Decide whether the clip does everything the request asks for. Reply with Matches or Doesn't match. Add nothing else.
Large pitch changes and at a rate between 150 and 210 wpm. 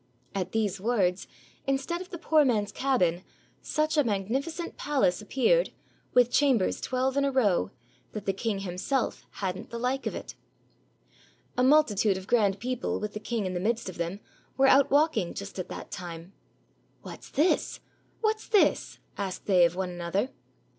Matches